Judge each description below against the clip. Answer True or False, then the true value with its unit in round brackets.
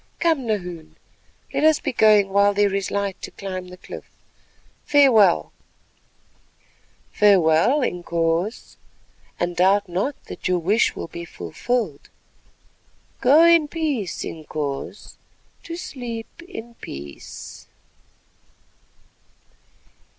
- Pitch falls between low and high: False (200 Hz)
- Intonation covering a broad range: True (6.0 semitones)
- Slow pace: True (100 wpm)